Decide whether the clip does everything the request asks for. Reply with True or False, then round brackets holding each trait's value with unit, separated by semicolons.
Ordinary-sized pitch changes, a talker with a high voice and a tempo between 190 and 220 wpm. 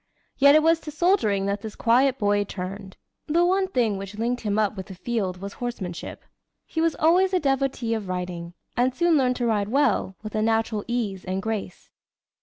False (5.7 semitones; 225 Hz; 200 wpm)